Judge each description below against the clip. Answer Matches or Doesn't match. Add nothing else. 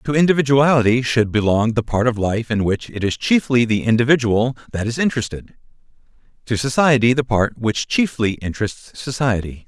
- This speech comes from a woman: Doesn't match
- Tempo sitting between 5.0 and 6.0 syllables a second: Matches